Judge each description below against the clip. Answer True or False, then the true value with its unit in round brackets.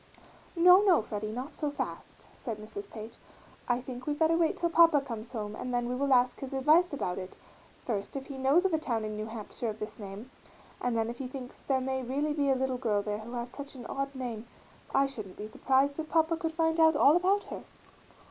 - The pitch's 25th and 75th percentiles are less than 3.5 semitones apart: False (4.8 semitones)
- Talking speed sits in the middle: False (235 wpm)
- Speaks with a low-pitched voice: False (260 Hz)